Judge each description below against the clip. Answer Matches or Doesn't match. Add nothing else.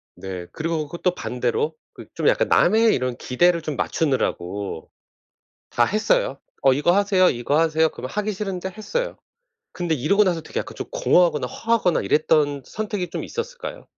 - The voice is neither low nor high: Matches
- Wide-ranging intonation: Matches